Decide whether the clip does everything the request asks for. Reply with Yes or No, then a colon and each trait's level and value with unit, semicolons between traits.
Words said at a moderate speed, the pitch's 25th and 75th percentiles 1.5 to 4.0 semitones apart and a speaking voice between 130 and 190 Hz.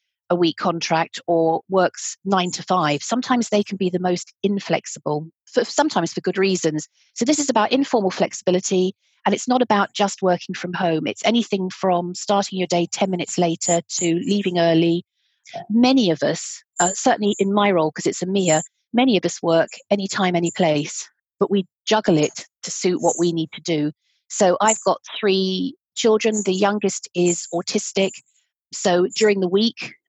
Yes: average, 175 wpm; average, 3.3 semitones; medium, 185 Hz